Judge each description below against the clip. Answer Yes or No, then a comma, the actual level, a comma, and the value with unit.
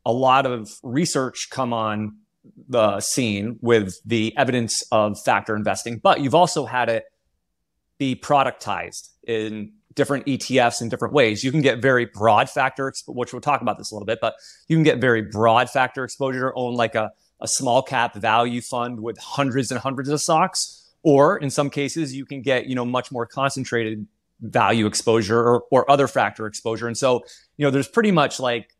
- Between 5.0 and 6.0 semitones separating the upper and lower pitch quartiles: No, average, 3.2 semitones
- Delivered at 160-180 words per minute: No, average, 190 wpm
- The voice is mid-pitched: No, low, 125 Hz